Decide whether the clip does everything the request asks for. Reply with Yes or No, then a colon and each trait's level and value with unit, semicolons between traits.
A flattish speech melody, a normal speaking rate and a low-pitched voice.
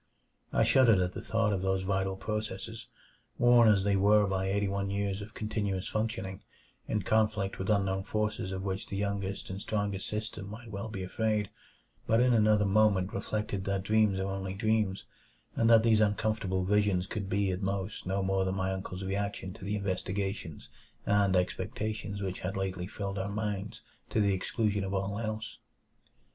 Yes: narrow, 1.9 semitones; average, 180 wpm; low, 100 Hz